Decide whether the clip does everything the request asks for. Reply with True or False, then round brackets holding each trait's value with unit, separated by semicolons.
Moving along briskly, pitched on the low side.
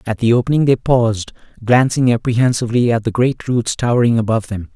False (175 wpm; 115 Hz)